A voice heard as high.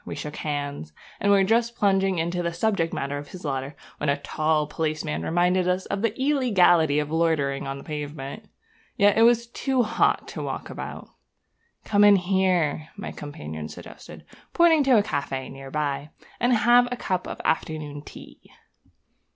No: medium, 165 Hz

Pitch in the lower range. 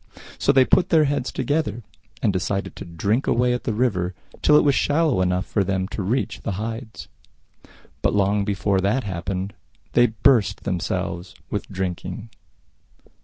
Yes: low, 105 Hz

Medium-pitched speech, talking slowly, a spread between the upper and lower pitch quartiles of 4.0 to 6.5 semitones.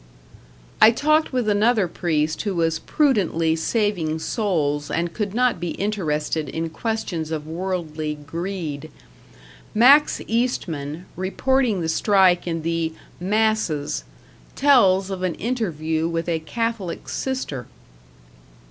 Yes: medium, 180 Hz; slow, 115 wpm; wide, 5.4 semitones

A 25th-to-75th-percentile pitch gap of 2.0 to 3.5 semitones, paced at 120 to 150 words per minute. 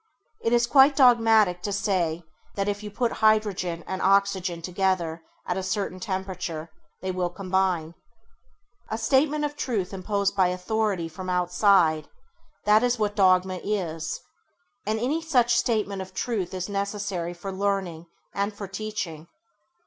Yes: average, 3.1 semitones; average, 145 wpm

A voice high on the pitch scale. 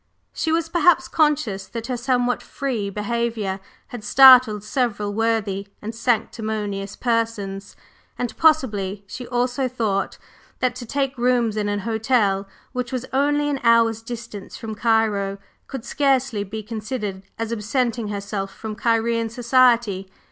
Yes: high, 230 Hz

